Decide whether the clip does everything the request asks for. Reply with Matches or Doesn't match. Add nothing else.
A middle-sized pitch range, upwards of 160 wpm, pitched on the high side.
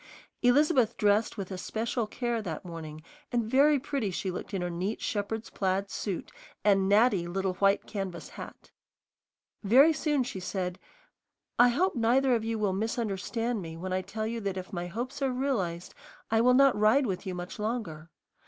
Matches